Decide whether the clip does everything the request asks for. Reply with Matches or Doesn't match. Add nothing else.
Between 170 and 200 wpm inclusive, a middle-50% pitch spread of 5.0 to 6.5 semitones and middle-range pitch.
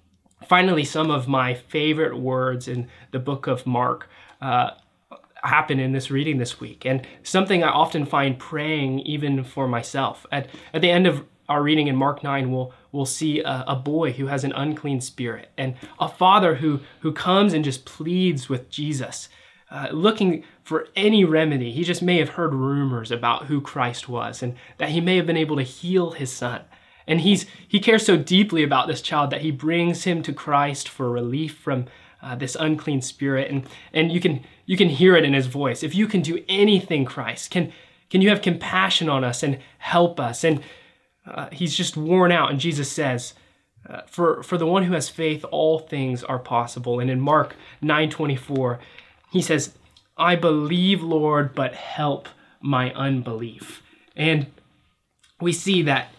Doesn't match